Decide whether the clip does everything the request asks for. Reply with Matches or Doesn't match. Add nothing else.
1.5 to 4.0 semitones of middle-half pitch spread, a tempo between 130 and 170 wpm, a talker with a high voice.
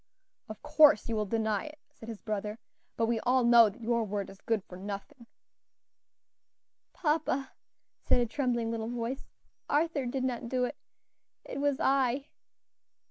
Matches